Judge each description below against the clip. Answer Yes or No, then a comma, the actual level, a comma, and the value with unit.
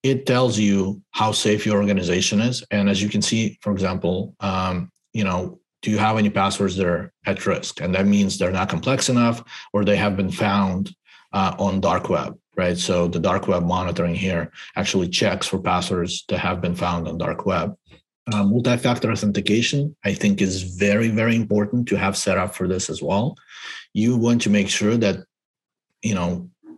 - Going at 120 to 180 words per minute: No, average, 195 wpm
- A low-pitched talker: Yes, low, 100 Hz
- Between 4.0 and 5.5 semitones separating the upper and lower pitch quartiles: No, average, 2.8 semitones